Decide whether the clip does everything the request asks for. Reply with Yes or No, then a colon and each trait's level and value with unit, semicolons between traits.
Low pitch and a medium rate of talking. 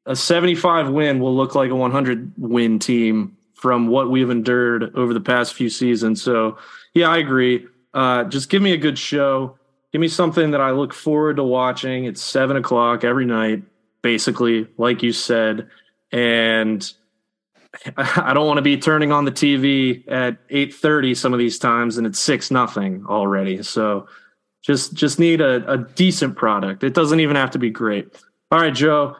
Yes: low, 130 Hz; average, 180 wpm